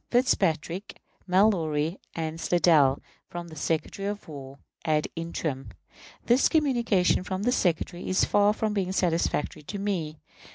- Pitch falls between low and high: Yes, medium, 175 Hz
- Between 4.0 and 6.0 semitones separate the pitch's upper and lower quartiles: Yes, average, 4.4 semitones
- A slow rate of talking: Yes, slow, 130 wpm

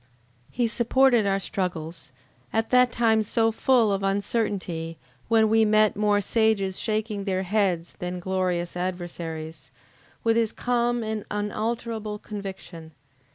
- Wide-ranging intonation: No, average, 3.4 semitones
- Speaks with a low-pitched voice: No, high, 210 Hz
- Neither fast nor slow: No, slow, 125 wpm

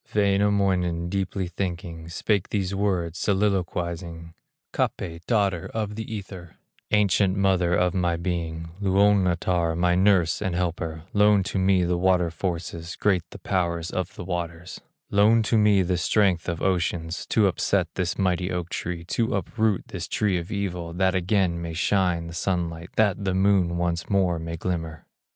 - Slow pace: No, average, 155 wpm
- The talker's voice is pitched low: Yes, very low, 90 Hz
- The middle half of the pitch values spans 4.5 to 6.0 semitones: No, narrow, 2.5 semitones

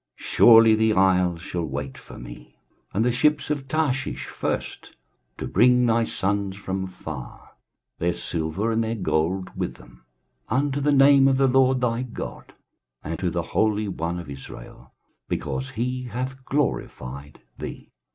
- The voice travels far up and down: Yes, wide, 6.7 semitones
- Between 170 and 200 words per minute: No, average, 155 wpm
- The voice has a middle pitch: No, low, 110 Hz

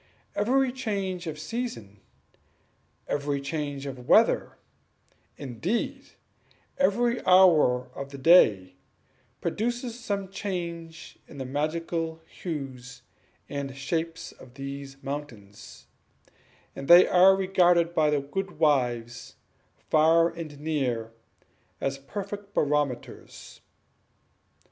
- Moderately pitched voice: Yes, medium, 155 Hz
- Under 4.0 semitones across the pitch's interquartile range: No, average, 5.3 semitones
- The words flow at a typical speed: No, slow, 100 wpm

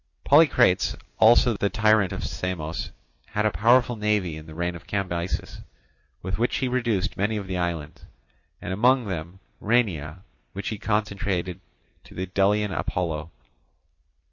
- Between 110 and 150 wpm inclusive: Yes, average, 140 wpm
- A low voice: Yes, low, 100 Hz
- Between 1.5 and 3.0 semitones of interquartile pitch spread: No, average, 3.8 semitones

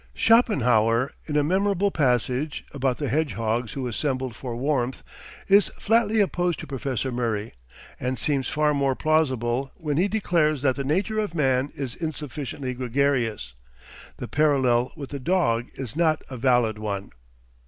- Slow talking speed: No, average, 150 wpm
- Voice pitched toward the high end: No, low, 135 Hz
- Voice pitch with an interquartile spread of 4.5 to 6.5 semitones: No, average, 4.0 semitones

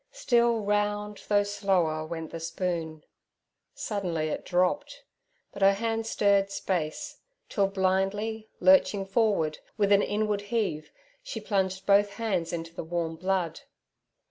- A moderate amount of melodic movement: Yes, average, 3.4 semitones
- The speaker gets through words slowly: Yes, slow, 130 wpm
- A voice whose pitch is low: No, high, 195 Hz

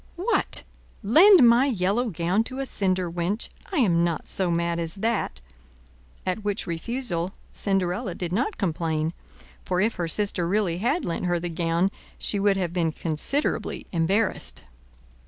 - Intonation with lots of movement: No, average, 4.6 semitones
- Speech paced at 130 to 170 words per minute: Yes, average, 155 wpm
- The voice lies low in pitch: No, medium, 185 Hz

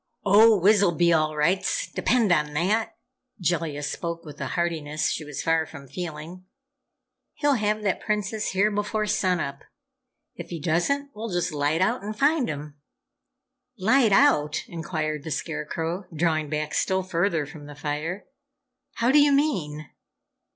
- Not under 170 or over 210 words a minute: No, average, 150 wpm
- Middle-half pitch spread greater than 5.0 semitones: Yes, wide, 5.4 semitones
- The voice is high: No, medium, 175 Hz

